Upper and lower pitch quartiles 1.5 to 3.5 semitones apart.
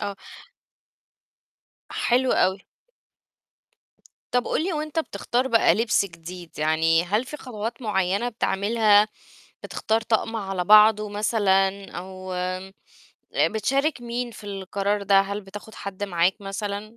Yes: average, 3.0 semitones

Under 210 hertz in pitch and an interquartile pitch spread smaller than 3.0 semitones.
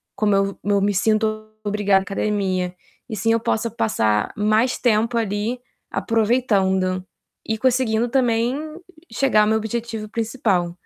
No: high, 215 Hz; narrow, 2.5 semitones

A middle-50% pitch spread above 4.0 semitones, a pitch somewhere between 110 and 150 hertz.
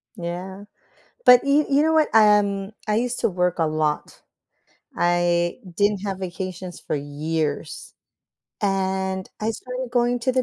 No: average, 5.2 semitones; high, 190 Hz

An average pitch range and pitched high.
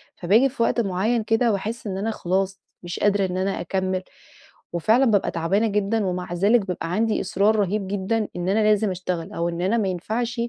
Yes: average, 3.1 semitones; high, 200 Hz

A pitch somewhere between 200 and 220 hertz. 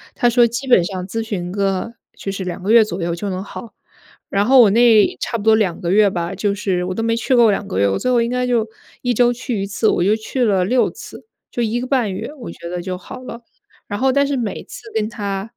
Yes: high, 215 Hz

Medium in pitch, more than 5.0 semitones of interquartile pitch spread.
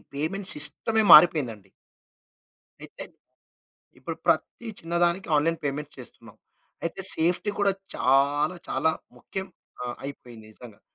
Yes: medium, 150 Hz; wide, 5.4 semitones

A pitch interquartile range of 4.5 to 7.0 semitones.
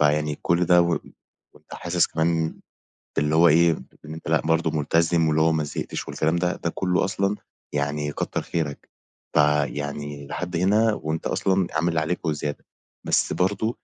No: narrow, 2.6 semitones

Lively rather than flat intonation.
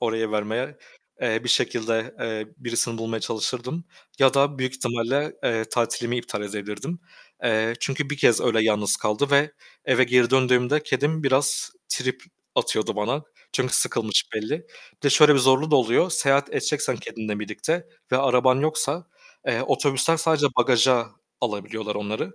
No: average, 3.9 semitones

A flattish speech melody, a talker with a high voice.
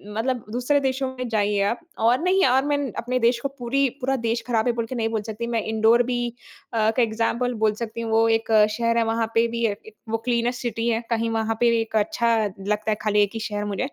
Yes: narrow, 1.8 semitones; high, 230 Hz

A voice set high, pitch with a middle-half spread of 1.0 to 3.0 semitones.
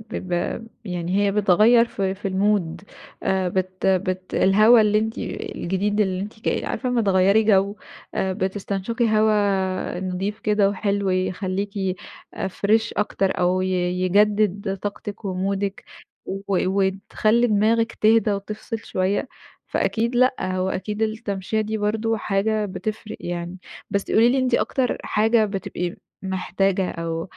Yes: high, 200 Hz; narrow, 2.4 semitones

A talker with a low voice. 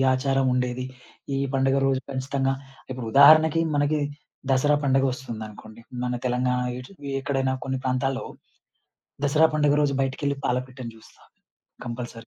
Yes: low, 130 Hz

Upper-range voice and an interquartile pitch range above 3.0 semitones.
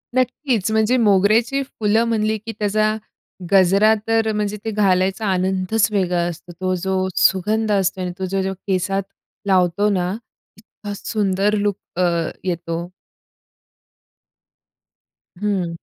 No: high, 200 Hz; narrow, 2.6 semitones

